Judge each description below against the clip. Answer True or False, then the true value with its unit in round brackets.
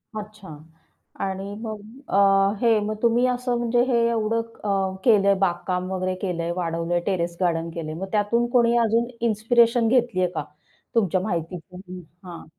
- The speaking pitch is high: True (200 Hz)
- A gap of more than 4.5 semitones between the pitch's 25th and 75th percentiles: False (4.2 semitones)